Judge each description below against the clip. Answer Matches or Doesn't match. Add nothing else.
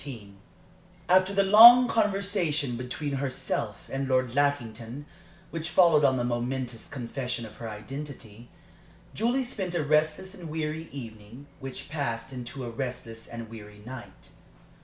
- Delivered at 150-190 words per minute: Doesn't match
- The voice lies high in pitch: Doesn't match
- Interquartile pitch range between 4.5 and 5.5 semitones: Matches